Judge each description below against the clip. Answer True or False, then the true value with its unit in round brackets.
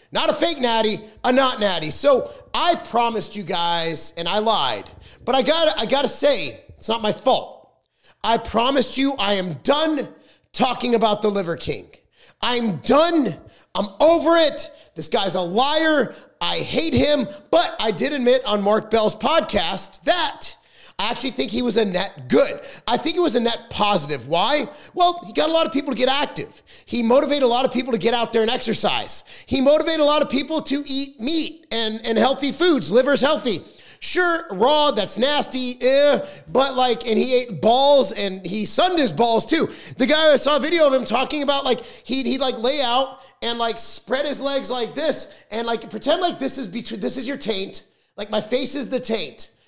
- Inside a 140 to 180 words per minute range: False (200 wpm)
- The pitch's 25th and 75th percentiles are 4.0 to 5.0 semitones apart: True (4.4 semitones)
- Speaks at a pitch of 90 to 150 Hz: False (255 Hz)